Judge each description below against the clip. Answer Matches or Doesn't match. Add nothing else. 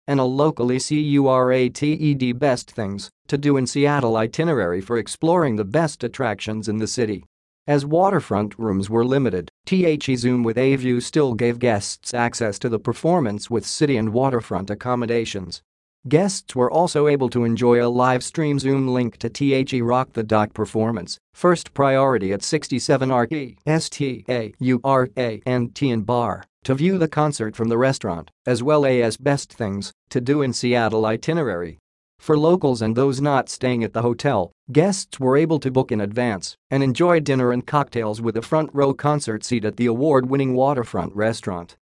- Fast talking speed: Doesn't match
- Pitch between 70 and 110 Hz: Doesn't match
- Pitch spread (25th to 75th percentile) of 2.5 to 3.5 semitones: Doesn't match